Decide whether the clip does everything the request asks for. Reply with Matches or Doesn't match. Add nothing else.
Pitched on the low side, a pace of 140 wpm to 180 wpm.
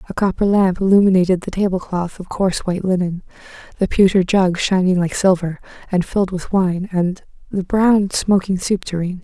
Doesn't match